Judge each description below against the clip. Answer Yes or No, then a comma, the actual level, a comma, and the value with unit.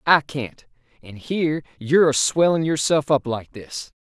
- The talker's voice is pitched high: No, low, 135 Hz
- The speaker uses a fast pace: No, average, 165 wpm